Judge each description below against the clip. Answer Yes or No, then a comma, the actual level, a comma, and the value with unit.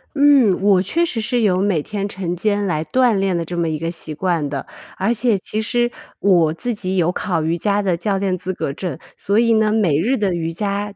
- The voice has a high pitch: Yes, high, 195 Hz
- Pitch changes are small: No, average, 3.9 semitones